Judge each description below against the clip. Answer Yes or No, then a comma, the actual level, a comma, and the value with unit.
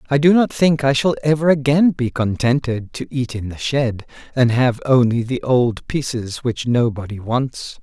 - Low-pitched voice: Yes, low, 130 Hz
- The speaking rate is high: No, average, 185 wpm